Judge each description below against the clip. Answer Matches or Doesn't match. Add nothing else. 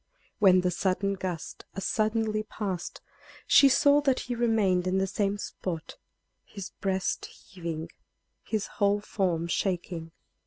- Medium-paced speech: Doesn't match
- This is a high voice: Matches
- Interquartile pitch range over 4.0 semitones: Doesn't match